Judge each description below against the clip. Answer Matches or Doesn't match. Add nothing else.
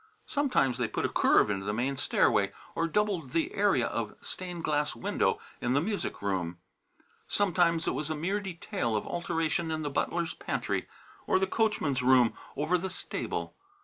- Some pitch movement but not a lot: Doesn't match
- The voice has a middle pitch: Matches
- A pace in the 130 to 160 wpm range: Doesn't match